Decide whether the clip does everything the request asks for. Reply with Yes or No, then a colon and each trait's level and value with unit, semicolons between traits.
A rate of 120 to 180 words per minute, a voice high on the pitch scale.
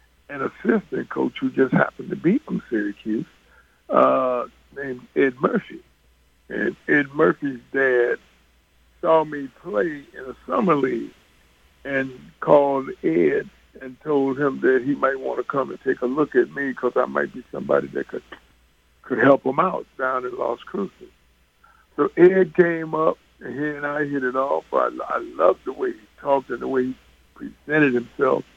No: average, 170 wpm; low, 135 Hz